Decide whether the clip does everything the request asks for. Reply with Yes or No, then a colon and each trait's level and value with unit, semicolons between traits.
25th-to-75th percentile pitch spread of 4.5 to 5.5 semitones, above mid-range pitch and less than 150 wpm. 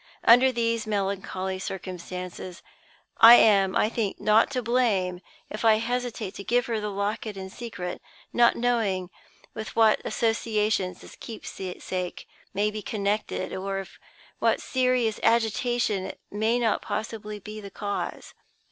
No: average, 3.0 semitones; high, 215 Hz; average, 140 wpm